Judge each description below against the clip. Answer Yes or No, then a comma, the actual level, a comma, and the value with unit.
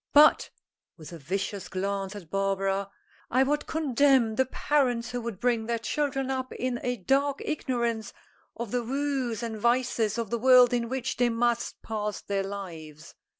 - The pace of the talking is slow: No, average, 165 wpm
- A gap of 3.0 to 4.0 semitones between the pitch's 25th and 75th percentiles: No, average, 4.5 semitones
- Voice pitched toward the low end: No, high, 235 Hz